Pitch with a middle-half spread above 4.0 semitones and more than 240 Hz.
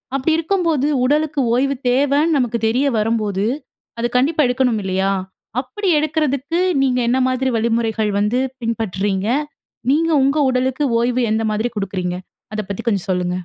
Yes: average, 4.7 semitones; very high, 250 Hz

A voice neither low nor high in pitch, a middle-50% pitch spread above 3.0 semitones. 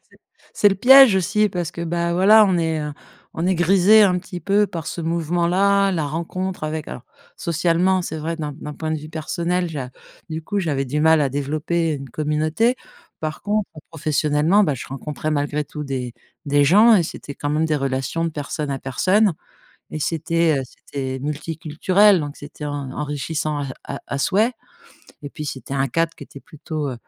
Yes: medium, 160 Hz; average, 3.6 semitones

